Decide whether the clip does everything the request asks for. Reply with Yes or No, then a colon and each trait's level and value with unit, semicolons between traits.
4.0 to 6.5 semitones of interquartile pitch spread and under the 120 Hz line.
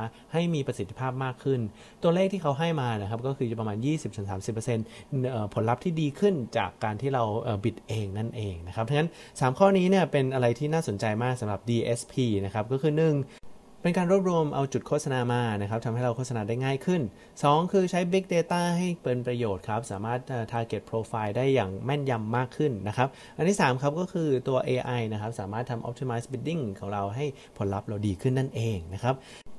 No: average, 4.7 semitones; low, 125 Hz